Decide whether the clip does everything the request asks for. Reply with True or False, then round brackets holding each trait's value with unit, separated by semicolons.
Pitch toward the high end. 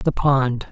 False (135 Hz)